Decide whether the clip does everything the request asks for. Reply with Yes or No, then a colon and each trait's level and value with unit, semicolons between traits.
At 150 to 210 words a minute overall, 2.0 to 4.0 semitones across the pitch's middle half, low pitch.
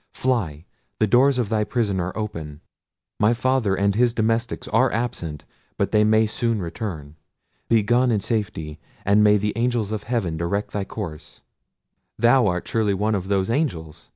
Yes: average, 170 wpm; average, 3.6 semitones; low, 105 Hz